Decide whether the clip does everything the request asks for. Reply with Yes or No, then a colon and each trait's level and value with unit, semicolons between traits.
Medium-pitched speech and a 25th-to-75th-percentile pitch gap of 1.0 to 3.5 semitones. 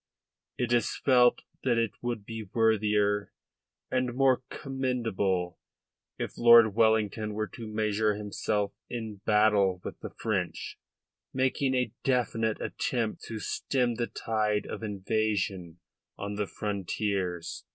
No: low, 110 Hz; narrow, 2.5 semitones